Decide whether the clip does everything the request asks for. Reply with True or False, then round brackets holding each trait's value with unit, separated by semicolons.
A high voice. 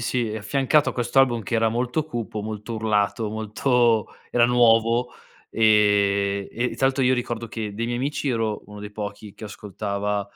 False (110 Hz)